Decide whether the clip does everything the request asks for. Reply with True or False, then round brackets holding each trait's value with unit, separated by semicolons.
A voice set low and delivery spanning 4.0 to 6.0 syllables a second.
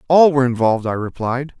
False (130 Hz; 6.7 syllables/s)